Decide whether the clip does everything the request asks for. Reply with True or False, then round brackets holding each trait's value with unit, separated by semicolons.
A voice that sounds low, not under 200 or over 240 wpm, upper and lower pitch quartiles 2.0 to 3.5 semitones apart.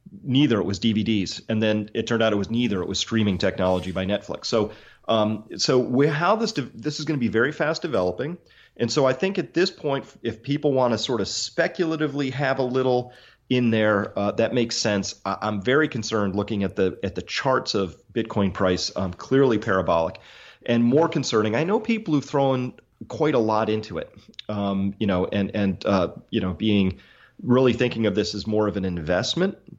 False (115 Hz; 205 wpm; 5.1 semitones)